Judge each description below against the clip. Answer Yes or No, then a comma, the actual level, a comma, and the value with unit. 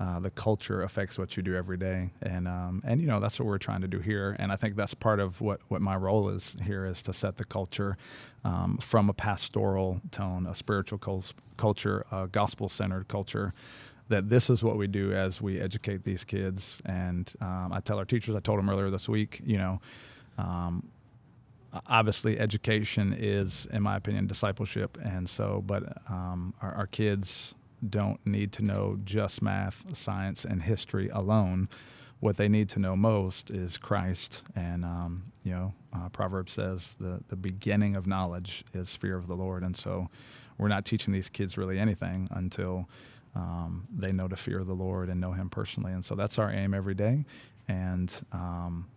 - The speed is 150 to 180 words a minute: No, average, 190 wpm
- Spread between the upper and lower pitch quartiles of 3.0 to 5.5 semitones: No, narrow, 2.5 semitones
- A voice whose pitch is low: Yes, low, 100 Hz